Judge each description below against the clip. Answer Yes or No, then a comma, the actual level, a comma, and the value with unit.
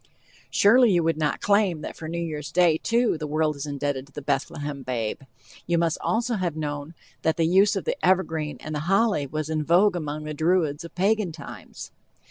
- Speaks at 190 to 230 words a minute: Yes, fast, 205 wpm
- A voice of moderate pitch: Yes, medium, 160 Hz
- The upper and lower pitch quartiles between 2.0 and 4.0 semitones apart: Yes, average, 3.7 semitones